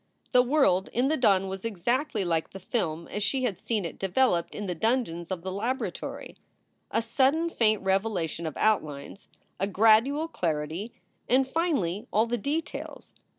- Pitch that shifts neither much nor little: No, wide, 5.8 semitones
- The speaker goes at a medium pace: Yes, average, 160 wpm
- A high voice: Yes, high, 215 Hz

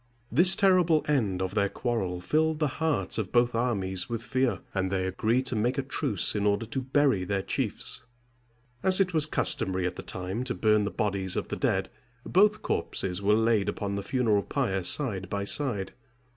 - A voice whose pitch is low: Yes, low, 110 Hz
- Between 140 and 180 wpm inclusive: No, average, 190 wpm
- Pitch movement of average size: No, wide, 5.8 semitones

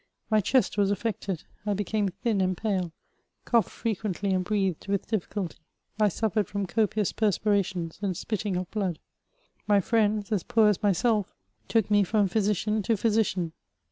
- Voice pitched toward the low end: No, high, 205 Hz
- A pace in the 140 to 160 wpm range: Yes, average, 155 wpm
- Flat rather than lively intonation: Yes, narrow, 2.3 semitones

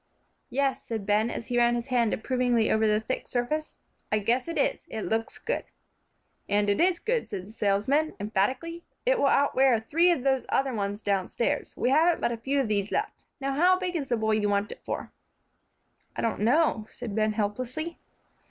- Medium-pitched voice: No, high, 240 Hz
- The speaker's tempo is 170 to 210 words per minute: Yes, average, 195 wpm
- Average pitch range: Yes, average, 4.9 semitones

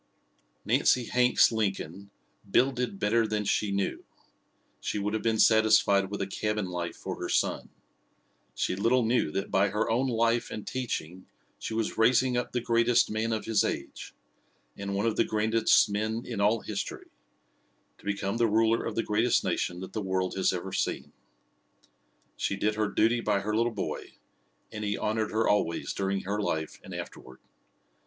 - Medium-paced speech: Yes, average, 175 wpm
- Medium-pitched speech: No, low, 105 Hz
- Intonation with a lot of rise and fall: No, narrow, 2.5 semitones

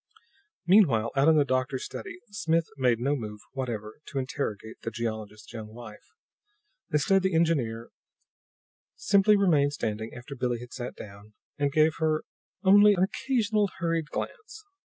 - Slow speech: No, average, 150 wpm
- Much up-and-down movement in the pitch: Yes, wide, 7.0 semitones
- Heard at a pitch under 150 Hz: Yes, medium, 140 Hz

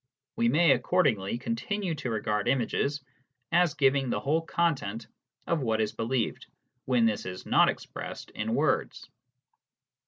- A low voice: Yes, low, 130 Hz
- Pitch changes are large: Yes, wide, 6.4 semitones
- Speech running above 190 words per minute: No, slow, 135 wpm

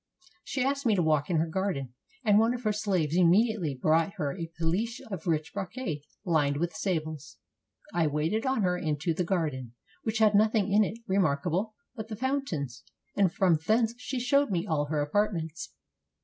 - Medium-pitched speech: Yes, medium, 180 Hz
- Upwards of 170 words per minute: Yes, average, 180 wpm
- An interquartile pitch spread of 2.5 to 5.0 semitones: No, wide, 5.6 semitones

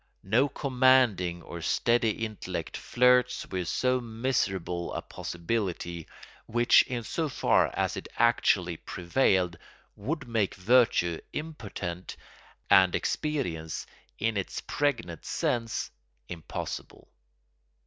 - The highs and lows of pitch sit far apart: Yes, wide, 6.1 semitones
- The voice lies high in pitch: No, low, 110 Hz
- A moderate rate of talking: No, slow, 100 wpm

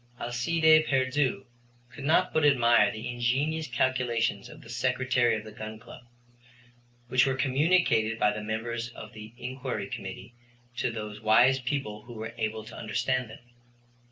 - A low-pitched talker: Yes, low, 120 Hz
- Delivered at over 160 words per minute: No, average, 155 wpm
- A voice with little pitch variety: No, average, 3.0 semitones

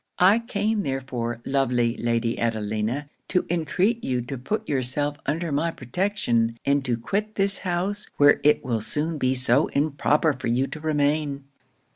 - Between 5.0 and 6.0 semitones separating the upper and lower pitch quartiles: Yes, wide, 5.5 semitones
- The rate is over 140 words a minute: Yes, average, 155 wpm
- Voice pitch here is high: No, medium, 140 Hz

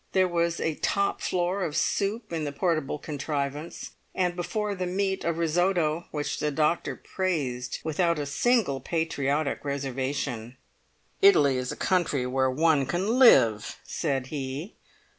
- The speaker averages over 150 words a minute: No, average, 140 wpm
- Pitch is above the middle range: No, medium, 160 Hz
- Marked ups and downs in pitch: No, average, 4.5 semitones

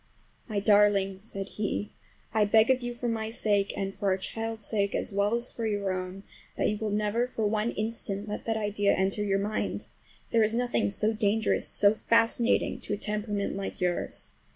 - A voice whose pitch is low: No, high, 210 Hz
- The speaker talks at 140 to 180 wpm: No, average, 195 wpm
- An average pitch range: No, narrow, 1.8 semitones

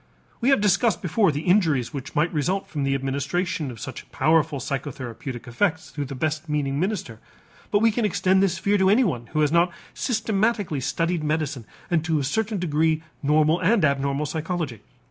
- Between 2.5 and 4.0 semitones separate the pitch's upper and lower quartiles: No, average, 5.2 semitones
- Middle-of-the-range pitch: Yes, medium, 155 Hz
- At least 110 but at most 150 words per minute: No, average, 180 wpm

